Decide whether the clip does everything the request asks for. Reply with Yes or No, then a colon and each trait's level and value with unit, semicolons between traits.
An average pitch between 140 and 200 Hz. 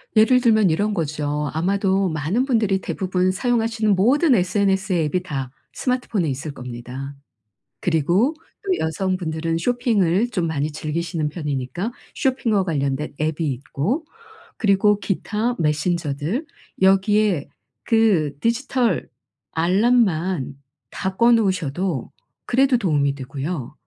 Yes: medium, 185 Hz